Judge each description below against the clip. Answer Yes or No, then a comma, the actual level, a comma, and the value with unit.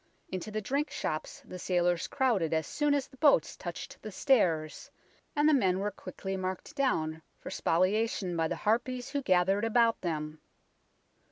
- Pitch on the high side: Yes, high, 195 Hz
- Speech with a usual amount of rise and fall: No, wide, 6.4 semitones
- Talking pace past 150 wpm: Yes, average, 165 wpm